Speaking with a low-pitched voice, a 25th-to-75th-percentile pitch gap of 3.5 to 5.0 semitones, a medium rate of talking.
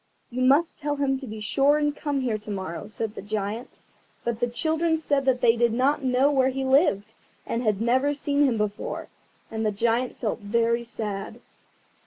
No: high, 245 Hz; average, 4.2 semitones; average, 195 wpm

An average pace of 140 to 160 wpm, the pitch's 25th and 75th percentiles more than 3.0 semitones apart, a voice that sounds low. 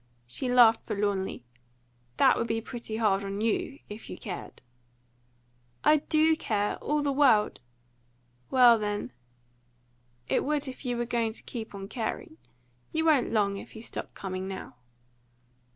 No: average, 150 wpm; average, 4.3 semitones; high, 225 Hz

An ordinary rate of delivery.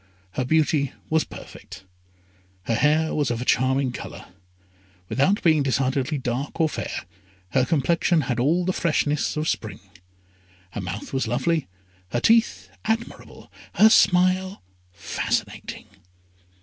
No: slow, 125 wpm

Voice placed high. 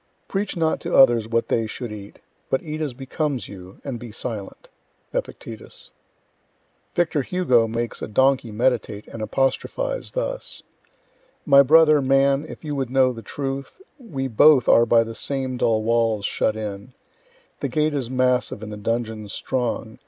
No: low, 130 Hz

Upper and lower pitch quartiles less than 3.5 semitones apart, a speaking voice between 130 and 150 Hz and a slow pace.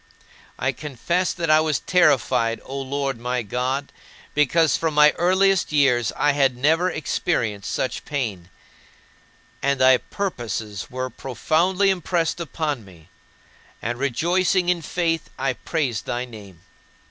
No: average, 5.2 semitones; medium, 140 Hz; slow, 130 wpm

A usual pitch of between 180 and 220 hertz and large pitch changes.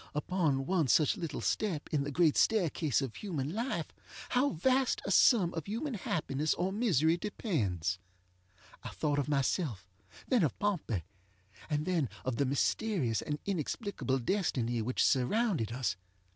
No: medium, 155 Hz; wide, 7.0 semitones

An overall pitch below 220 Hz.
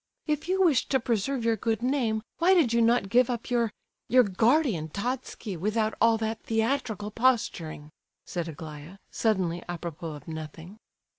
No: high, 225 Hz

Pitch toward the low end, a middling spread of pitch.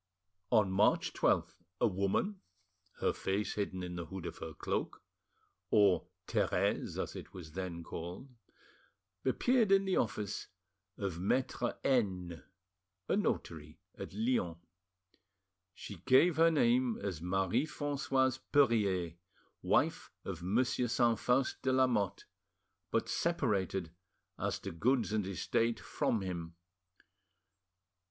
No: low, 105 Hz; wide, 6.1 semitones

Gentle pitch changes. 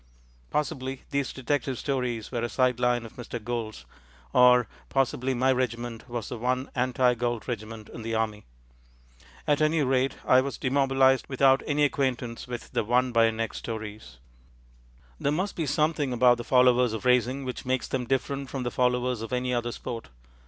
Yes: narrow, 2.0 semitones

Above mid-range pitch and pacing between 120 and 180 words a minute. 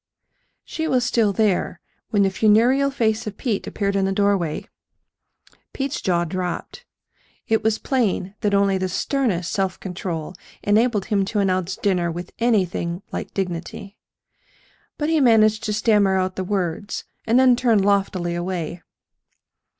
Yes: high, 200 Hz; average, 145 wpm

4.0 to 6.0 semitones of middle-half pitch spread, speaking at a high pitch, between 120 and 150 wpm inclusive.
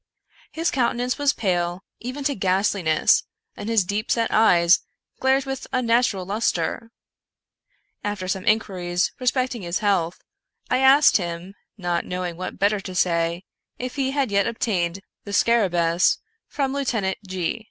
Yes: wide, 5.5 semitones; high, 205 Hz; average, 140 wpm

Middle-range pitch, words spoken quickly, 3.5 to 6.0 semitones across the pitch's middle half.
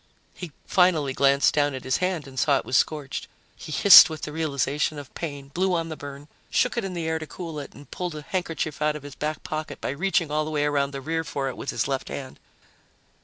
No: medium, 150 Hz; fast, 245 wpm; narrow, 2.6 semitones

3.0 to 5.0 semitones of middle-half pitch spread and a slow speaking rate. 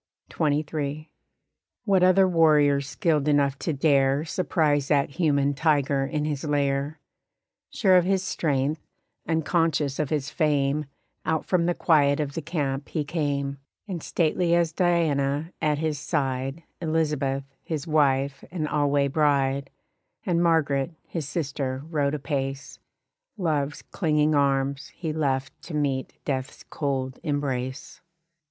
No: narrow, 2.6 semitones; slow, 130 wpm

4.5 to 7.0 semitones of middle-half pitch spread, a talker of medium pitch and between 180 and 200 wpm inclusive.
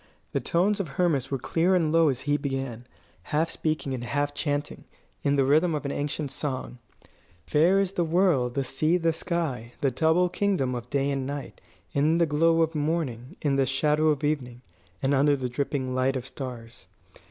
No: average, 3.6 semitones; medium, 145 Hz; average, 190 wpm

